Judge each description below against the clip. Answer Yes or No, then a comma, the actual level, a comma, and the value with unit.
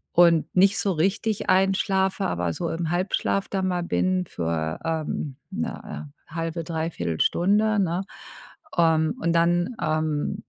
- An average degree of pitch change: Yes, average, 3.2 semitones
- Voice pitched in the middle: Yes, medium, 170 Hz